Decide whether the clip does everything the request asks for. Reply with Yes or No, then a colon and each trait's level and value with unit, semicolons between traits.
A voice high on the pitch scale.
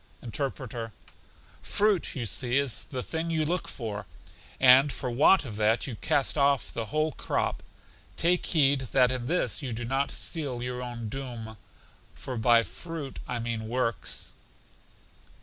No: low, 130 Hz